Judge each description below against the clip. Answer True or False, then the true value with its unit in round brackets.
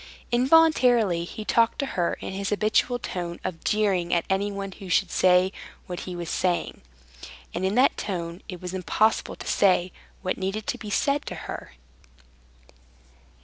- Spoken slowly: False (160 wpm)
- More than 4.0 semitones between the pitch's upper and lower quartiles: False (3.2 semitones)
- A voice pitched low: False (195 Hz)